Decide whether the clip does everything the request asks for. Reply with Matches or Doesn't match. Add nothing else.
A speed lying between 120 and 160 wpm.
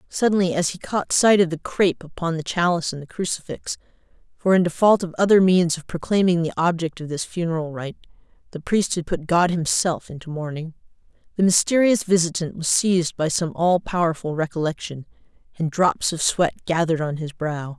Doesn't match